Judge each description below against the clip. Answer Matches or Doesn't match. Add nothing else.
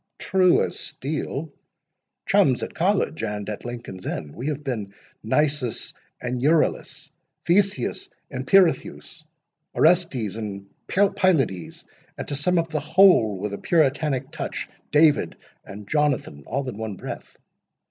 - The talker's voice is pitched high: Doesn't match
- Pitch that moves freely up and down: Matches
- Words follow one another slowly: Matches